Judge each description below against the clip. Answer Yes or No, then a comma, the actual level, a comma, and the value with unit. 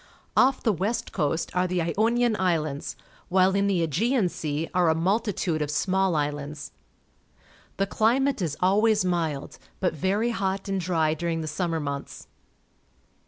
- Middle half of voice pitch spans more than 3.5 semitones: Yes, average, 4.0 semitones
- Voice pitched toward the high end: No, medium, 180 Hz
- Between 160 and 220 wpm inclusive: No, average, 150 wpm